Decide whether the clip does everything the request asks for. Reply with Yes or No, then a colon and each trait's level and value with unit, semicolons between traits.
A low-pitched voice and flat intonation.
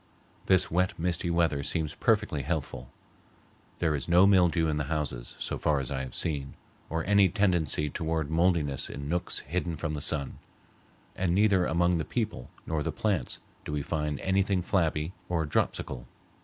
No: very low, 80 Hz; average, 3.5 semitones